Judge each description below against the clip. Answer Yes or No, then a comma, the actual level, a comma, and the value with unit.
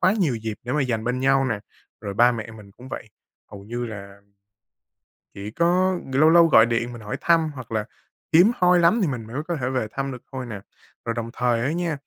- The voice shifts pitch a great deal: Yes, wide, 6.0 semitones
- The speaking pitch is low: Yes, low, 125 Hz